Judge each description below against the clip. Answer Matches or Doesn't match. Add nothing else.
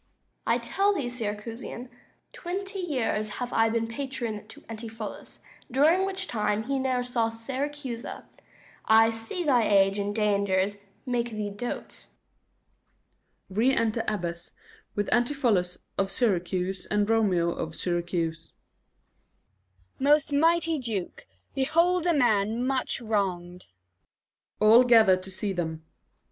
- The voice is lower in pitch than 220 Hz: Doesn't match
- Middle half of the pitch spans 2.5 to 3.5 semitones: Doesn't match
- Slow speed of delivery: Matches